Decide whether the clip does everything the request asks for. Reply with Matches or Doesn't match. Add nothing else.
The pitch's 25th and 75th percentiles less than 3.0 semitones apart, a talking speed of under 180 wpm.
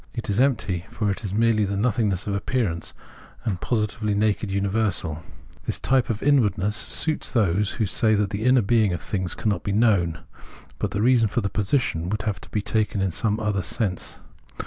Doesn't match